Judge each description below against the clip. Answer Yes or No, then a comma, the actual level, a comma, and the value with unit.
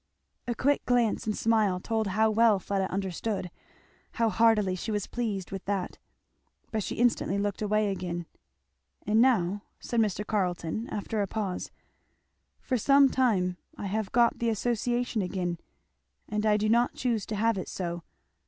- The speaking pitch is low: No, high, 210 Hz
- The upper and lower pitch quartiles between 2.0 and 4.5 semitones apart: Yes, average, 3.1 semitones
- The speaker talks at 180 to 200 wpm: No, average, 160 wpm